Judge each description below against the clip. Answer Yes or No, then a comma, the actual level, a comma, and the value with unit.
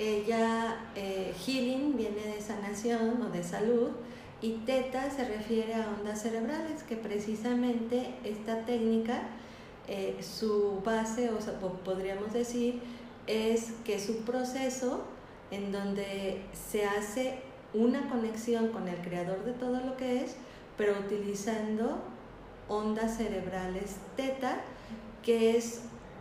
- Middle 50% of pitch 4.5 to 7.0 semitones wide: No, average, 2.8 semitones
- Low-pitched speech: No, high, 225 Hz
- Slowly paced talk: Yes, slow, 120 wpm